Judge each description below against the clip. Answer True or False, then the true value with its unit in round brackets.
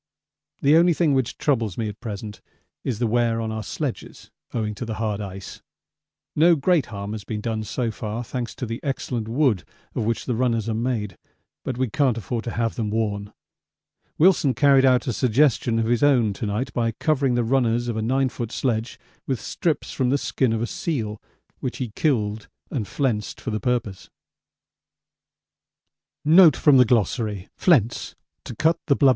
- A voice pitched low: True (115 Hz)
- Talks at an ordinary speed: True (165 wpm)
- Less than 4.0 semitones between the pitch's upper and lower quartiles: True (3.2 semitones)